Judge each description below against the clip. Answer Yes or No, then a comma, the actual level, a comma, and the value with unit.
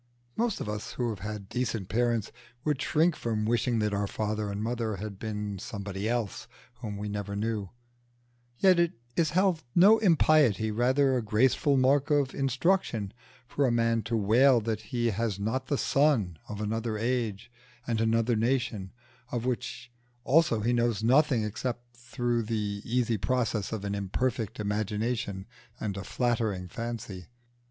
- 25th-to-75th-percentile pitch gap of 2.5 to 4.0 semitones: Yes, average, 3.3 semitones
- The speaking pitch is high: No, low, 115 Hz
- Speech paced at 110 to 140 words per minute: No, average, 160 wpm